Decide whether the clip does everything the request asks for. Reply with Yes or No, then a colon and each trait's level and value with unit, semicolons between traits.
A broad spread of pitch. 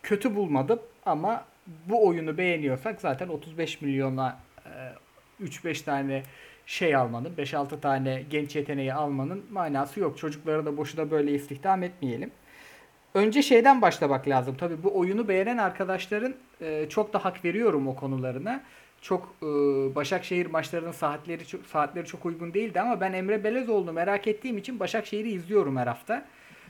Yes: wide, 5.7 semitones